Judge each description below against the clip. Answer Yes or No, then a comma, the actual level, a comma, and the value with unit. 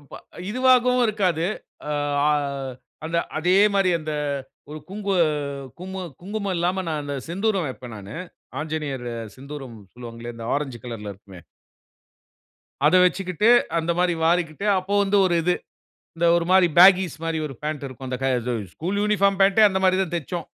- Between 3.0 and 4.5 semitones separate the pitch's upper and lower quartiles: No, average, 5.1 semitones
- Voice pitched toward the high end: No, medium, 170 Hz